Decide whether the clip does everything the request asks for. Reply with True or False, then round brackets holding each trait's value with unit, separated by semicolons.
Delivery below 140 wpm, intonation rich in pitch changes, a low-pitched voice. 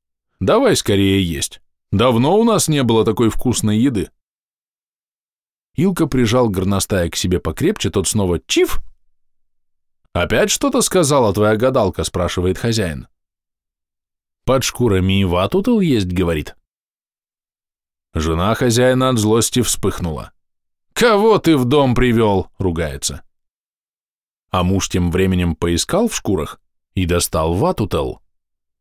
True (110 wpm; 6.4 semitones; 100 Hz)